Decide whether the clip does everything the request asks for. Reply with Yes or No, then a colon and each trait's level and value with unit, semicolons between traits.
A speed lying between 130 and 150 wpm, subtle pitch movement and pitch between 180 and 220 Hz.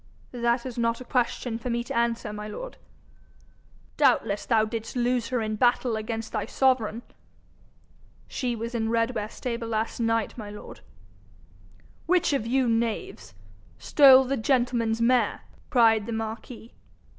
No: average, 145 wpm; narrow, 1.9 semitones; high, 235 Hz